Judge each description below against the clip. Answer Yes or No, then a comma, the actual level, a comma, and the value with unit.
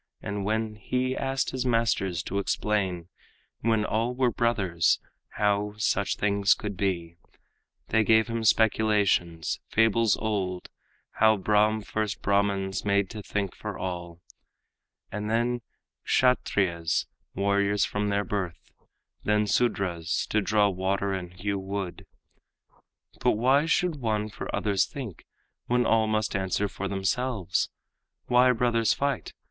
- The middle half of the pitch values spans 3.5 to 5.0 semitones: No, narrow, 2.6 semitones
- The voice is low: Yes, low, 105 Hz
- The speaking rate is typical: No, slow, 130 wpm